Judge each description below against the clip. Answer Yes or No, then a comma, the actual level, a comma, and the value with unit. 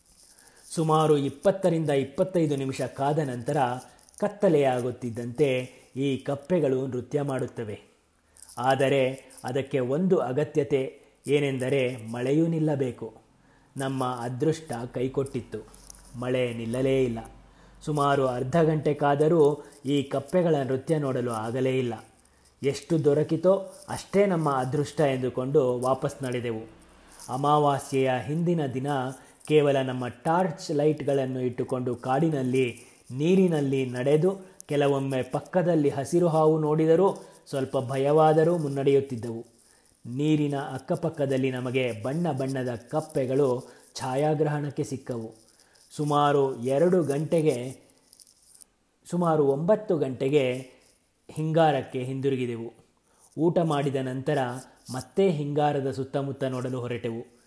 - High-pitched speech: No, low, 135 Hz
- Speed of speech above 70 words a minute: Yes, average, 90 wpm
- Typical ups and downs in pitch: Yes, average, 3.1 semitones